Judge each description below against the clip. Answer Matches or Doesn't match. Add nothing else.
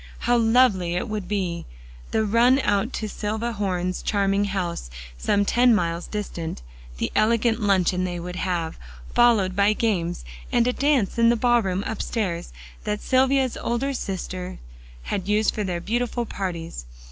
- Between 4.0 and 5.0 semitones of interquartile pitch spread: Matches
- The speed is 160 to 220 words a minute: Doesn't match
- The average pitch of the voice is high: Matches